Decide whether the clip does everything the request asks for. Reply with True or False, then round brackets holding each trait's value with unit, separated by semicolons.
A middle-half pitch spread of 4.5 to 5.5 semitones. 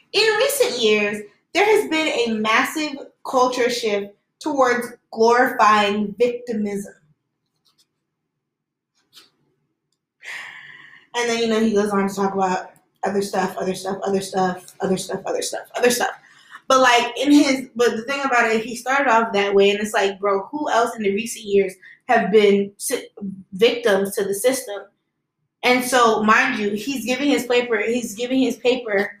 False (3.8 semitones)